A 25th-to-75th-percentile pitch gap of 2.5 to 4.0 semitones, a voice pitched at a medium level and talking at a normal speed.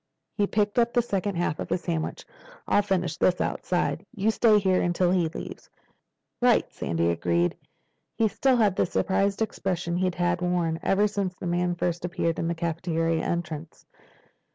Yes: average, 2.9 semitones; medium, 180 Hz; average, 170 wpm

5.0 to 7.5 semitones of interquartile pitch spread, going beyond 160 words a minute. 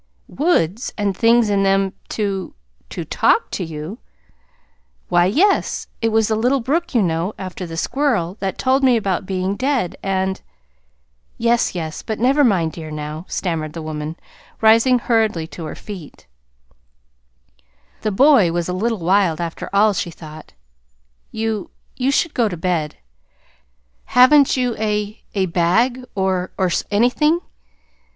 No: wide, 5.4 semitones; average, 145 wpm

